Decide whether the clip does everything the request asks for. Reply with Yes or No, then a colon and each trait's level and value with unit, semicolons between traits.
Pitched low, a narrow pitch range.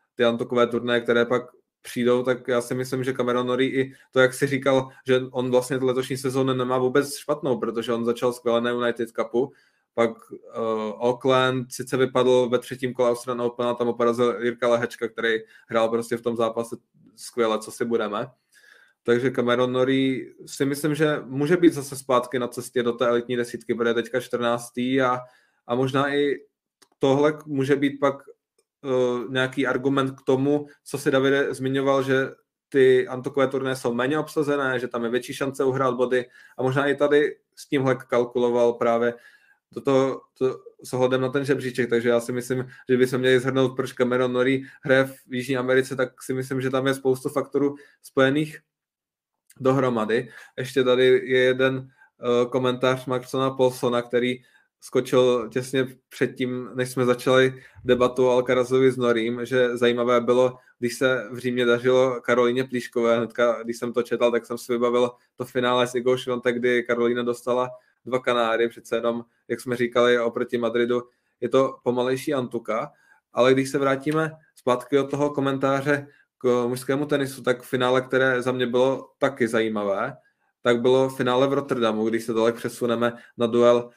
Yes: low, 125 Hz; narrow, 1.7 semitones